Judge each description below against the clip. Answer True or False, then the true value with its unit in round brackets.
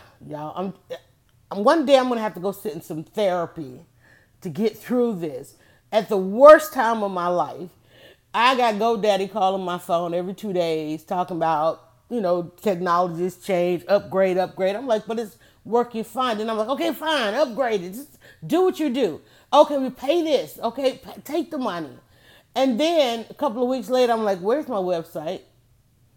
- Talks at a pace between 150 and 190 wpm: True (180 wpm)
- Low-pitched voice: False (200 Hz)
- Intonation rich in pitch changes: True (6.3 semitones)